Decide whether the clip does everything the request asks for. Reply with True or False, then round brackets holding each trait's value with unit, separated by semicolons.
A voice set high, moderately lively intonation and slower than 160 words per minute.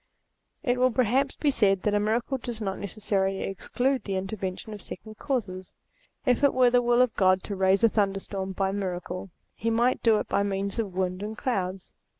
False (205 Hz; 3.9 semitones; 195 wpm)